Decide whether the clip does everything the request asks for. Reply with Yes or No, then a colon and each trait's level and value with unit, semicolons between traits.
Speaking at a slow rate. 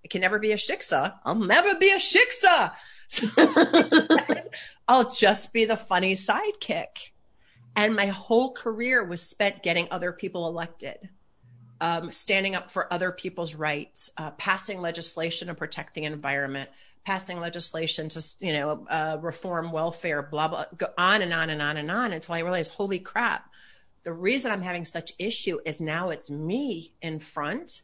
No: average, 165 wpm